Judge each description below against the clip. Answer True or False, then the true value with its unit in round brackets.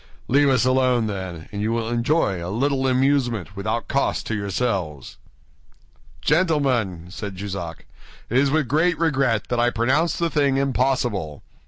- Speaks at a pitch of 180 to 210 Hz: False (120 Hz)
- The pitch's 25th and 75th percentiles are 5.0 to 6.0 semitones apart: True (5.4 semitones)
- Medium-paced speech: True (150 wpm)